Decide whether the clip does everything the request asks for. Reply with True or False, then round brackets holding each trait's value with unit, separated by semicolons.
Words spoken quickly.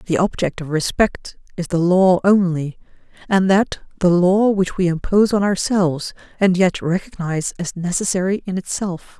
False (155 wpm)